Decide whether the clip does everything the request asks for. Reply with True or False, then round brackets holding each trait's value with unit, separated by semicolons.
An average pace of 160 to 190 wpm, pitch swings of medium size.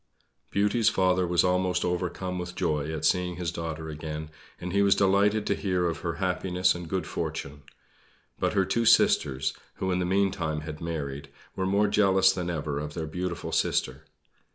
True (175 wpm; 3.0 semitones)